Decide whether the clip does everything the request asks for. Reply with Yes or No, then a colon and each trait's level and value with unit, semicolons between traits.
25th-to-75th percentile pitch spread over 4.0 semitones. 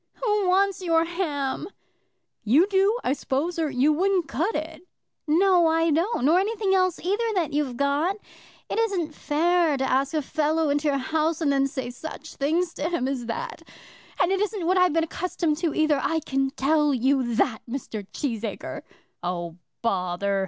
Yes: average, 4.8 semitones